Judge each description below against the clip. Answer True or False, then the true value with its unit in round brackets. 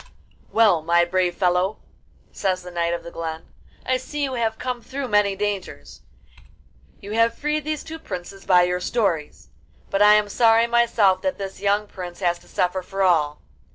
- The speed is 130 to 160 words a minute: False (180 wpm)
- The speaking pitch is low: False (195 Hz)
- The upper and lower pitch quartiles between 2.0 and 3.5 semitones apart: False (4.5 semitones)